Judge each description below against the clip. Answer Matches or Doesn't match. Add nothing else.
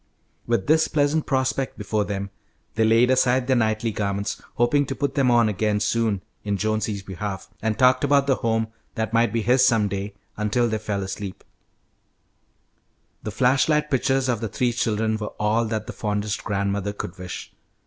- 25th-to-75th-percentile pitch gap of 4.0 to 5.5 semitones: Doesn't match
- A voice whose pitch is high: Doesn't match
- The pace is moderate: Matches